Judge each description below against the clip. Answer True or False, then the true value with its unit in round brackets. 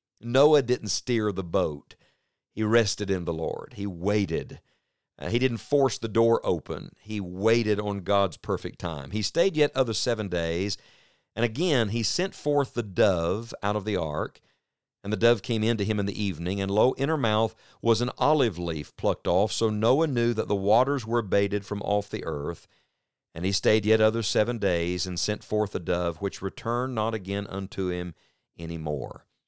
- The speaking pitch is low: True (105 Hz)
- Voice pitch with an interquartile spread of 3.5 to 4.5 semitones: False (3.1 semitones)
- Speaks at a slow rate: False (190 wpm)